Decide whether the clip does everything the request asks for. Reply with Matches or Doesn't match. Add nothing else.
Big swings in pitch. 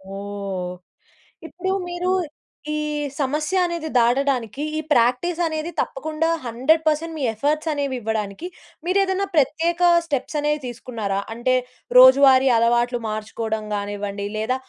Matches